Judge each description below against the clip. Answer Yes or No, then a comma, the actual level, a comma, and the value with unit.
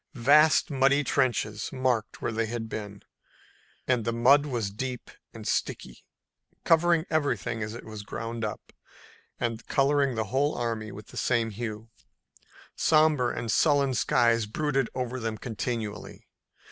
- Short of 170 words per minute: Yes, slow, 135 wpm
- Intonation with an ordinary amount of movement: Yes, average, 3.7 semitones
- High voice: No, low, 120 Hz